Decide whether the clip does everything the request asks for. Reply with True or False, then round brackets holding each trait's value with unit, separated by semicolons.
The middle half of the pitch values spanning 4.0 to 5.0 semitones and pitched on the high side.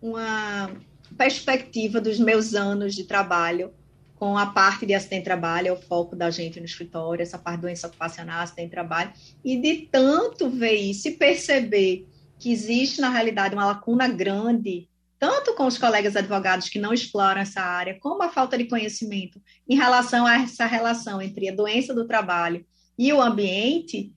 True (4.7 semitones; 205 Hz)